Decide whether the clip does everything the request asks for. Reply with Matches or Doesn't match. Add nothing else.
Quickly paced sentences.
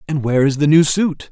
Matches